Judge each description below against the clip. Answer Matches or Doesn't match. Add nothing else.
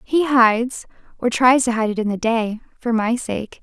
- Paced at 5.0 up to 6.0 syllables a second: Doesn't match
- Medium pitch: Doesn't match